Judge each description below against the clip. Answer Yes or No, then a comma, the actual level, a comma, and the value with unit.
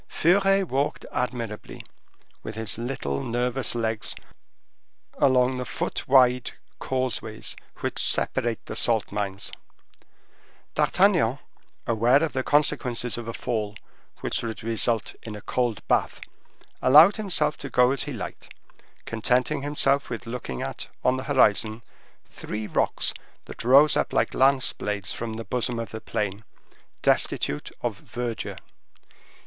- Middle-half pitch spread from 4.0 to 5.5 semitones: No, average, 3.1 semitones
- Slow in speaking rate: Yes, slow, 130 wpm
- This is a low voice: Yes, low, 120 Hz